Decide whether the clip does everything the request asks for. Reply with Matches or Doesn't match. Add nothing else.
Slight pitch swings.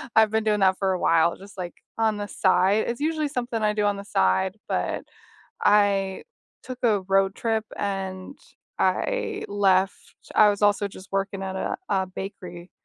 Matches